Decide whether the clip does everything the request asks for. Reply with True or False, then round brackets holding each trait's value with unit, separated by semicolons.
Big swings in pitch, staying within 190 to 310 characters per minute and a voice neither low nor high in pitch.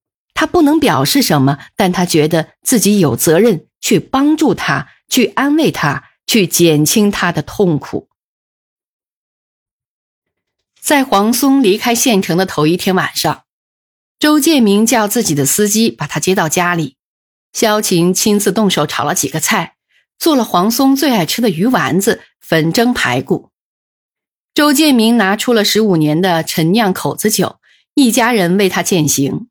False (6.9 semitones; 220 characters per minute; 195 Hz)